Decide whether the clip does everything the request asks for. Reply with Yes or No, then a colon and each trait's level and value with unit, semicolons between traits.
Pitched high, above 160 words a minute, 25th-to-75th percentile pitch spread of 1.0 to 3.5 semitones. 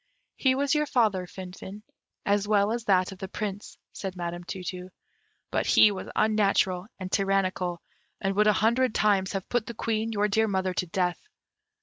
Yes: high, 195 Hz; average, 185 wpm; narrow, 2.6 semitones